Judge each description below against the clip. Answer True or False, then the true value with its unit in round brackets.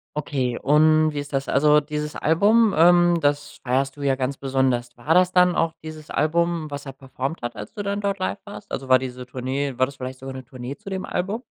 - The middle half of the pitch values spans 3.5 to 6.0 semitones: True (4.3 semitones)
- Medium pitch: True (145 Hz)